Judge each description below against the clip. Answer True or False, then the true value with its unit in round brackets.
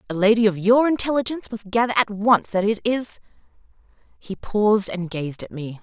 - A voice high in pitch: True (215 Hz)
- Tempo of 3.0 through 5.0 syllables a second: False (5.5 syllables/s)